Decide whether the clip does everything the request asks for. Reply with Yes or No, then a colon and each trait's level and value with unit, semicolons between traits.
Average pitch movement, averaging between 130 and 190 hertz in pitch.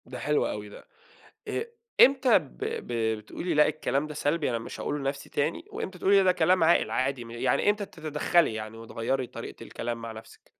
No: wide, 6.8 semitones; medium, 140 Hz